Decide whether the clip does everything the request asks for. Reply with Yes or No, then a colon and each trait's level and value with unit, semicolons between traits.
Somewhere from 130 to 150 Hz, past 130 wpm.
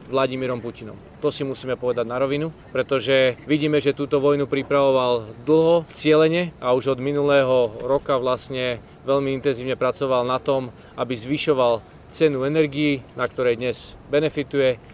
Yes: low, 135 Hz; average, 140 wpm